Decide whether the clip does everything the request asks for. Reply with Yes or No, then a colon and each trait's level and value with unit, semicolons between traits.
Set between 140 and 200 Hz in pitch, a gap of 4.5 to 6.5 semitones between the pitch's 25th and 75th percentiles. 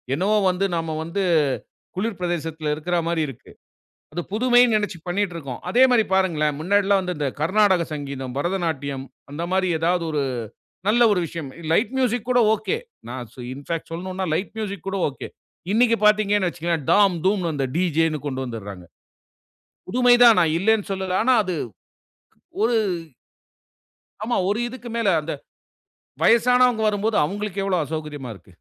Yes: medium, 185 Hz; average, 5.0 semitones